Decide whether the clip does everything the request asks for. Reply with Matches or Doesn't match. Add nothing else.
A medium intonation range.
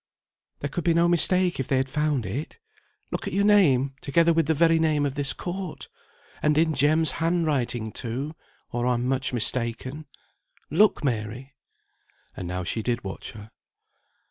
Matches